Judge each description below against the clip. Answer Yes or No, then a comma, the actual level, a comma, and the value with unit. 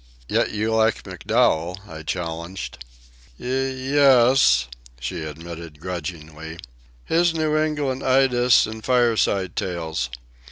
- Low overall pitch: Yes, low, 100 Hz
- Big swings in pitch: Yes, wide, 8.1 semitones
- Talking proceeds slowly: Yes, slow, 105 wpm